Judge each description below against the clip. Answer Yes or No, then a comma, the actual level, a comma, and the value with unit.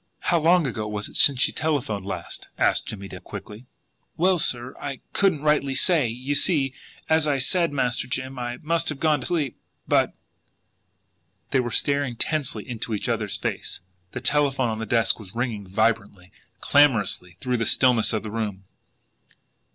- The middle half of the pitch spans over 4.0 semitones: Yes, average, 5.0 semitones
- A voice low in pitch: Yes, low, 125 Hz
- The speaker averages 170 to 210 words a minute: Yes, average, 175 wpm